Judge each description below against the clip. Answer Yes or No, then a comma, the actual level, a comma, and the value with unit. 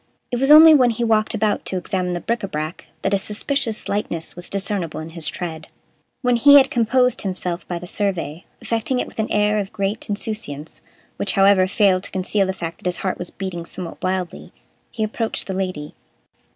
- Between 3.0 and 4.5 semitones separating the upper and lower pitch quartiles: Yes, average, 3.7 semitones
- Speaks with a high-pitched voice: Yes, high, 195 Hz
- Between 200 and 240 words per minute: Yes, fast, 205 wpm